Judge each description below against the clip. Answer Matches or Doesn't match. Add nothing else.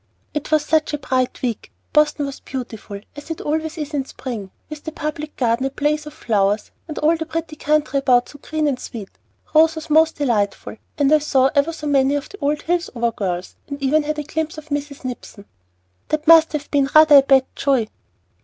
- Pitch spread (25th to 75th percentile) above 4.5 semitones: Doesn't match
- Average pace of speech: Doesn't match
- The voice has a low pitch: Doesn't match